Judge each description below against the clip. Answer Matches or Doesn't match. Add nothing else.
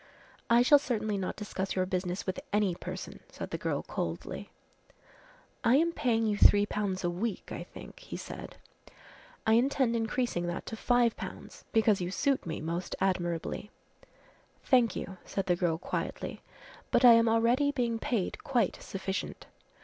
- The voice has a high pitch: Matches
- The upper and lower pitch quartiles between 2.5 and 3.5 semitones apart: Doesn't match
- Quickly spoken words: Doesn't match